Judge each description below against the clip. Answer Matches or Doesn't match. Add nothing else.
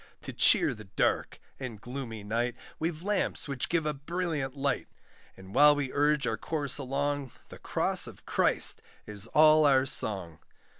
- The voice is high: Doesn't match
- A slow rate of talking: Doesn't match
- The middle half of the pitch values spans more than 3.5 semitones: Matches